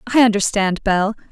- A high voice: Yes, high, 210 Hz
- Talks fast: No, slow, 135 wpm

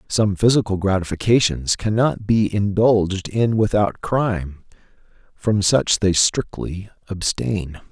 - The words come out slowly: Yes, slow, 105 wpm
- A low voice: Yes, low, 100 Hz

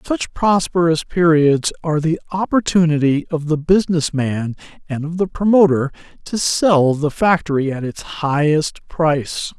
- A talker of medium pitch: Yes, medium, 160 Hz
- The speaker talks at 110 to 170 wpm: Yes, average, 140 wpm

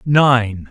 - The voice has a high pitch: No, low, 120 Hz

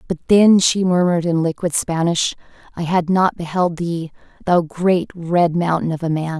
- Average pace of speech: Yes, average, 180 wpm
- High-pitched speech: No, medium, 170 Hz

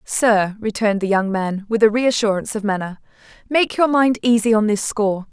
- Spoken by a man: No, female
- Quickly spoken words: No, average, 190 wpm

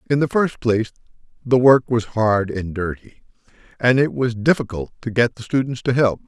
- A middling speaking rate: Yes, average, 190 wpm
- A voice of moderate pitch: No, low, 120 Hz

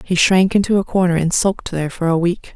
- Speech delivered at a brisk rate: Yes, fast, 260 wpm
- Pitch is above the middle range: No, medium, 180 Hz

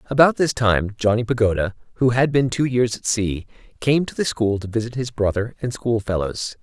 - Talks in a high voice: No, low, 115 Hz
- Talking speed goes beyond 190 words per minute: Yes, average, 200 wpm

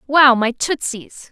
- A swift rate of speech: No, slow, 135 wpm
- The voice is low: No, very high, 260 Hz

